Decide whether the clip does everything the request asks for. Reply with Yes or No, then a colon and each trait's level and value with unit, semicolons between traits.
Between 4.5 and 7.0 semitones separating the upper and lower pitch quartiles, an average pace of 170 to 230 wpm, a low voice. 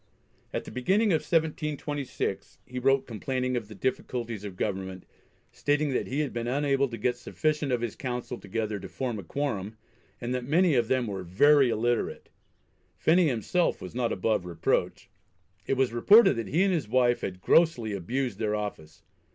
Yes: average, 4.9 semitones; average, 175 wpm; low, 125 Hz